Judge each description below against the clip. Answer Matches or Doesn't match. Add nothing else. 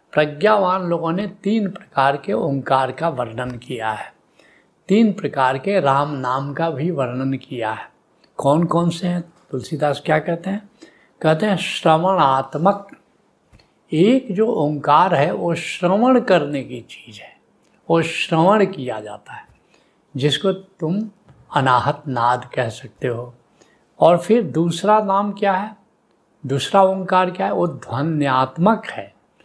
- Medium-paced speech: Matches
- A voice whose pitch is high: Doesn't match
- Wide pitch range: Matches